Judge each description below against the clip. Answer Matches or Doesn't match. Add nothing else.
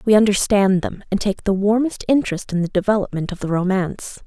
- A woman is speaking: Matches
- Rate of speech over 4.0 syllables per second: Matches